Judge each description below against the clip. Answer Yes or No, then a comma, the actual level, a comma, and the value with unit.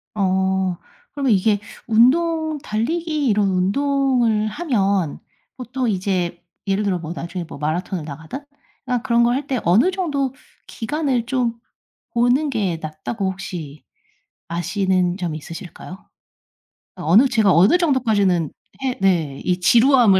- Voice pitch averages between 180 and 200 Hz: No, high, 210 Hz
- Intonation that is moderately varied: No, wide, 6.2 semitones